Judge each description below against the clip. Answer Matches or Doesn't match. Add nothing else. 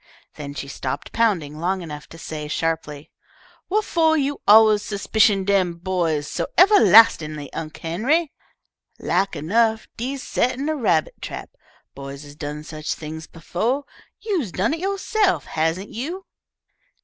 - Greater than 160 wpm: Doesn't match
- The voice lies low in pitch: Doesn't match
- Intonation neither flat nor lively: Doesn't match